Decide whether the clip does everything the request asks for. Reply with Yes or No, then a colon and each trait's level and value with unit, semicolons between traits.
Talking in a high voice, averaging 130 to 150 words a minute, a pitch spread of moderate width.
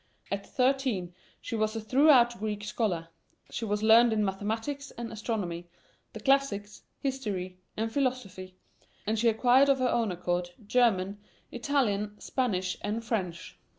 Yes: high, 220 Hz; average, 140 wpm; average, 3.9 semitones